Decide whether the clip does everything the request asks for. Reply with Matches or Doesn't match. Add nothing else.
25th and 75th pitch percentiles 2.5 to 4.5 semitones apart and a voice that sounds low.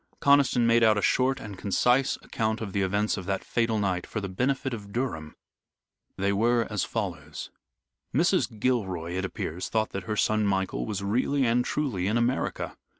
Matches